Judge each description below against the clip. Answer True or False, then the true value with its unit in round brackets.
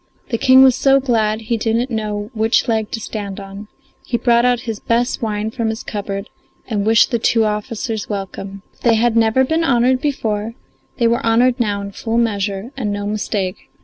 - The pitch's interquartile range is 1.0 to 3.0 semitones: True (2.5 semitones)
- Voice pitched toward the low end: False (225 Hz)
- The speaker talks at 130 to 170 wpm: False (195 wpm)